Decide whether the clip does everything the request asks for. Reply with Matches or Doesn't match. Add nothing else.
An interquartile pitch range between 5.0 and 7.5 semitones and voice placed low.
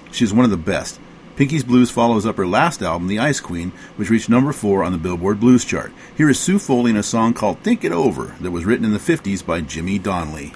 Matches